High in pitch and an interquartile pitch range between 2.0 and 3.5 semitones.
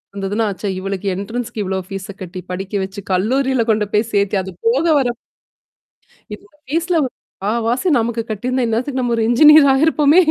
No: high, 230 Hz; average, 4.8 semitones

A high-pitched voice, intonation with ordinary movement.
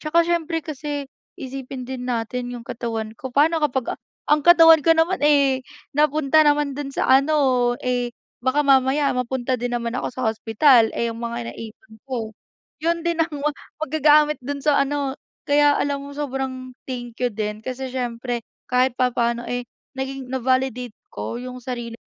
Yes: very high, 260 Hz; average, 3.1 semitones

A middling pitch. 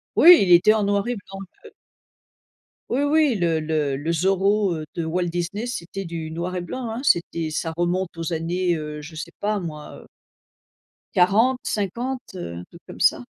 Yes: medium, 180 Hz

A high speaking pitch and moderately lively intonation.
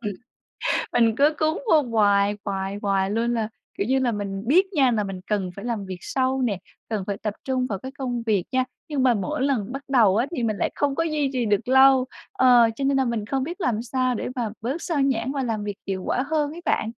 Yes: high, 240 Hz; average, 4.4 semitones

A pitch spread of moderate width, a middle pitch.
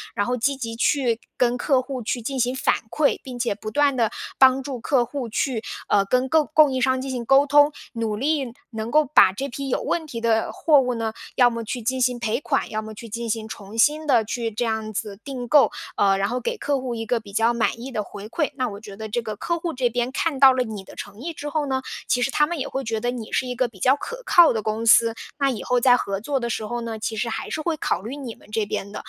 No: average, 3.5 semitones; high, 245 Hz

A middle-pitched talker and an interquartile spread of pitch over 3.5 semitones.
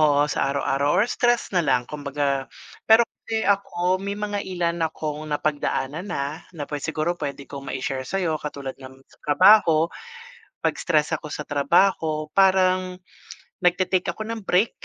Yes: medium, 160 Hz; average, 4.5 semitones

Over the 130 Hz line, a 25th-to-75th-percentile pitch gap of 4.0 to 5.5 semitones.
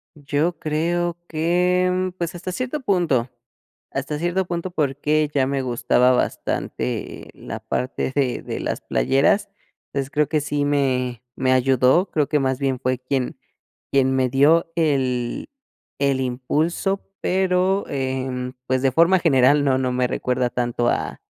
Yes: medium, 140 Hz; average, 4.7 semitones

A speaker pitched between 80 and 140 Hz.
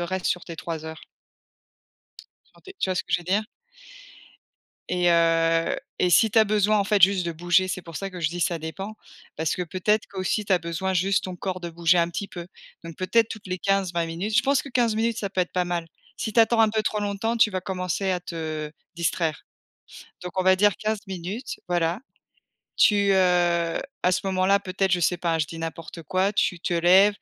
No: medium, 185 Hz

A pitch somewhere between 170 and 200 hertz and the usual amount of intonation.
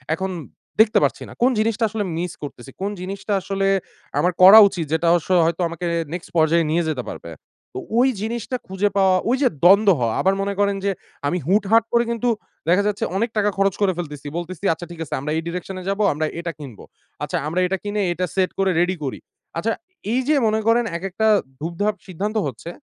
Yes: high, 190 Hz; average, 3.7 semitones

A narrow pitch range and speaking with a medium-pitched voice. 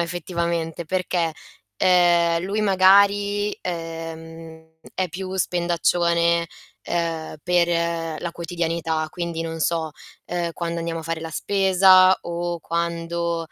Yes: narrow, 1.4 semitones; medium, 170 Hz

